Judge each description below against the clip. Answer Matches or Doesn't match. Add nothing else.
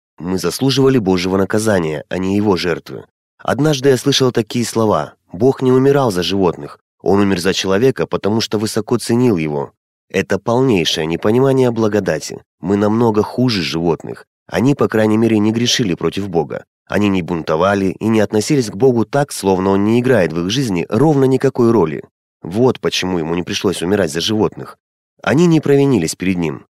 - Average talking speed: Doesn't match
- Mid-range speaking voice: Doesn't match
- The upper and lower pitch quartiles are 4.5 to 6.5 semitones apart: Matches